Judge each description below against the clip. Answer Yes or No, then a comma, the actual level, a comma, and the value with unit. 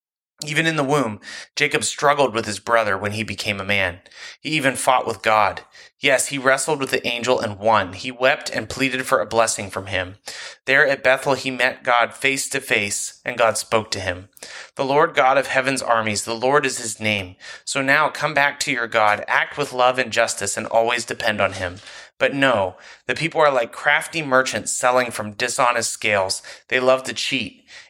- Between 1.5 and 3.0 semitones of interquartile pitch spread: No, average, 4.0 semitones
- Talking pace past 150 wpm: Yes, average, 200 wpm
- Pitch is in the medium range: No, low, 125 Hz